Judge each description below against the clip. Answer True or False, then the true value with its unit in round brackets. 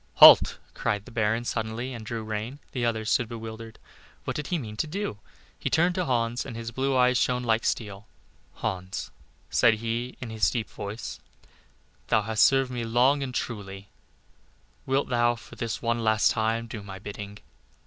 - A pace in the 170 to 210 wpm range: True (180 wpm)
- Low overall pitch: True (115 Hz)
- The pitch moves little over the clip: True (2.2 semitones)